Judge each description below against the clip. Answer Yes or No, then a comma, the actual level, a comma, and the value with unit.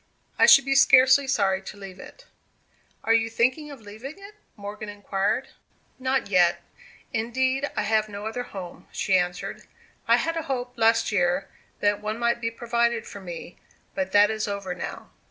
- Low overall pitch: No, high, 220 Hz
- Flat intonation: No, average, 4.2 semitones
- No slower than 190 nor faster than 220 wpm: No, average, 175 wpm